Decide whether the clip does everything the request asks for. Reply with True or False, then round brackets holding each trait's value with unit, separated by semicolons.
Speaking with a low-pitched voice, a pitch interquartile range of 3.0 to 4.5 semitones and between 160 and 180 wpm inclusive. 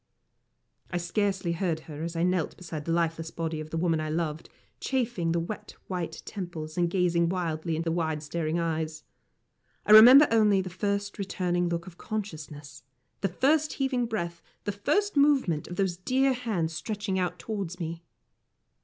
False (175 Hz; 3.8 semitones; 170 wpm)